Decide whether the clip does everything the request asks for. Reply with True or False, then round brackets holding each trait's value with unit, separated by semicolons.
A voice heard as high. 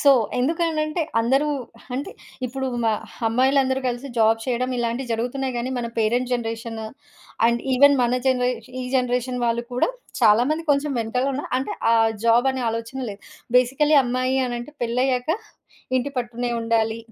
True (250 Hz)